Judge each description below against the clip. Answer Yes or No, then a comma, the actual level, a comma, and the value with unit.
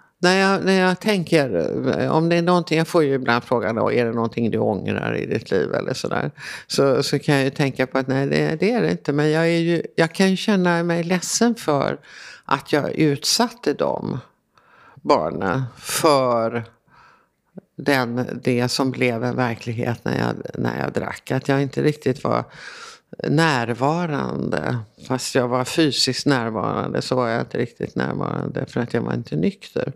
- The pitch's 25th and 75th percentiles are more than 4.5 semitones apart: Yes, wide, 5.6 semitones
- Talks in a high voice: No, medium, 140 Hz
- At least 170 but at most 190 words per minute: Yes, average, 180 wpm